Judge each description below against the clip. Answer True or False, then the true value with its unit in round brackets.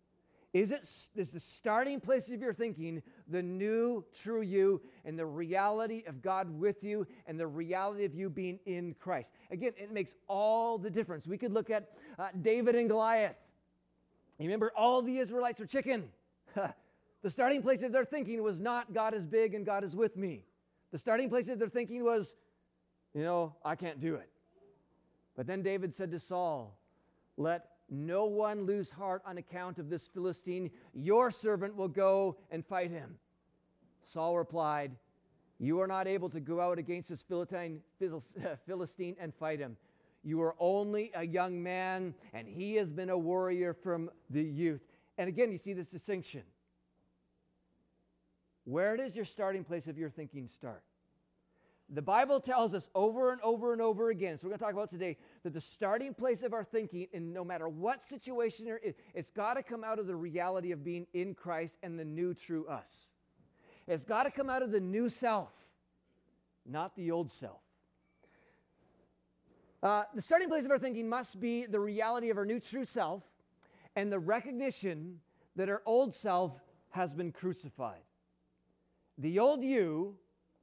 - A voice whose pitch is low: False (185 Hz)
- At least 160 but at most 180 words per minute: True (175 wpm)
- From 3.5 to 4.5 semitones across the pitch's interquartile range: False (5.1 semitones)